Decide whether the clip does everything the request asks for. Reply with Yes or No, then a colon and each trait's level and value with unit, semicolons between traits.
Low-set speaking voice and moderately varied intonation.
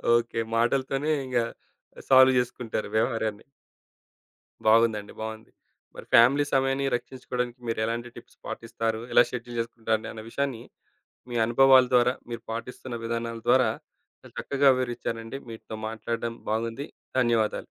No: low, 120 Hz; narrow, 2.2 semitones